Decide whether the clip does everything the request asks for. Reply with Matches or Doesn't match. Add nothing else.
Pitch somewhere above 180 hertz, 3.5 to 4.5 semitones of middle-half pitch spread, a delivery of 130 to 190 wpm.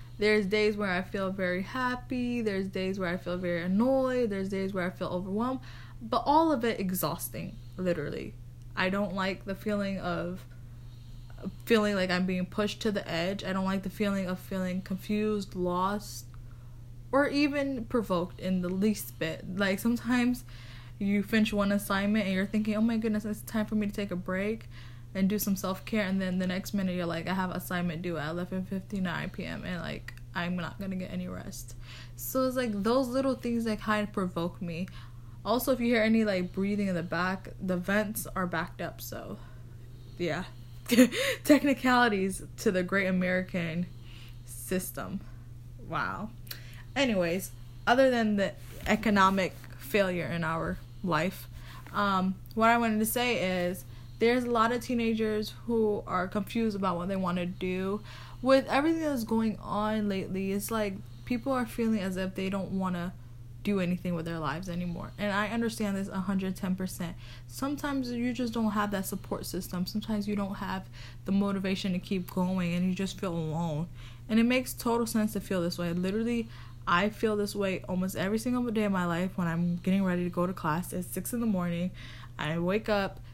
Matches